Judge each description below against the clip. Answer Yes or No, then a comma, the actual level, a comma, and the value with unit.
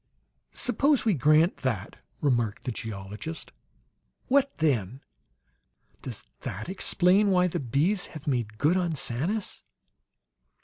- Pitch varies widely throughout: Yes, wide, 7.7 semitones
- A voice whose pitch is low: No, medium, 155 Hz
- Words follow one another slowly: Yes, slow, 115 wpm